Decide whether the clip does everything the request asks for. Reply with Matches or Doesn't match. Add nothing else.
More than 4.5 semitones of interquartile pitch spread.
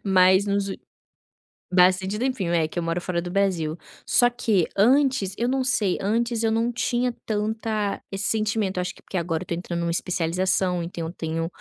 Doesn't match